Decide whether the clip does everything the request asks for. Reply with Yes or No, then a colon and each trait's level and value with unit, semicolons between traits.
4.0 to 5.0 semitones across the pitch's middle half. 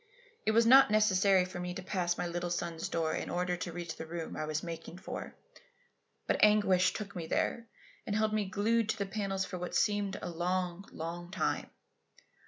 No: average, 3.0 semitones